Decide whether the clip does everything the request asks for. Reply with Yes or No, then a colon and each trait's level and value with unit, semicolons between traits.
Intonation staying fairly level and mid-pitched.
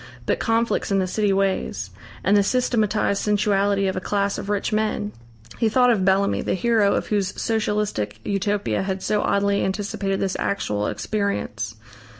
No: narrow, 1.7 semitones; high, 200 Hz